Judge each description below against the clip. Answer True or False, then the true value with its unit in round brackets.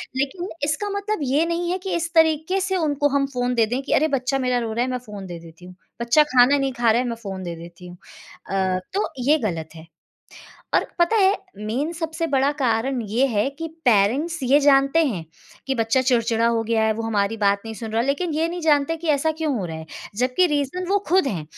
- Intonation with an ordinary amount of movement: False (6.2 semitones)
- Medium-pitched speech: False (260 Hz)